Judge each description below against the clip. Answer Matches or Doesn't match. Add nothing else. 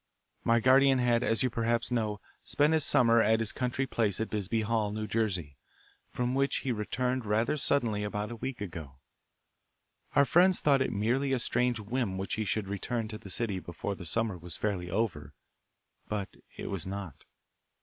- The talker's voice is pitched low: Matches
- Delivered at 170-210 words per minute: Matches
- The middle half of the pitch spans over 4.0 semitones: Doesn't match